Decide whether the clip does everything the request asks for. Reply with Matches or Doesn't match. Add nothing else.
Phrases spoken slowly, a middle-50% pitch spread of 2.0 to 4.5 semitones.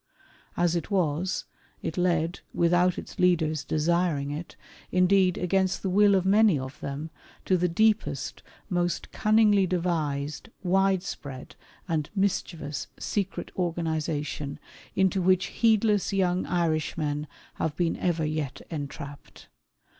Matches